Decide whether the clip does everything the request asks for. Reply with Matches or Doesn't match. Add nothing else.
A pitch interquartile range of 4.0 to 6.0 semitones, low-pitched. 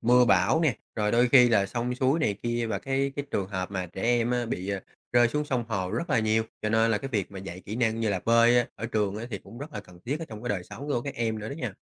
Doesn't match